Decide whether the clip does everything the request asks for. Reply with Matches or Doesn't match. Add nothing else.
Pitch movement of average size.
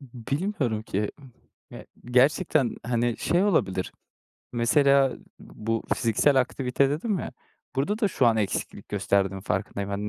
Matches